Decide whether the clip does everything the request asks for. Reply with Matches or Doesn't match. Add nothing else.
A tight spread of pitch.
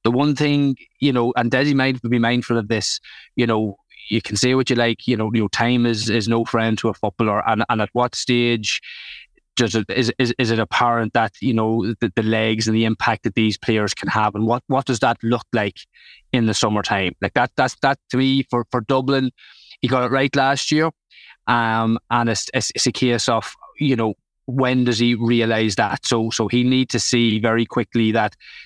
Matches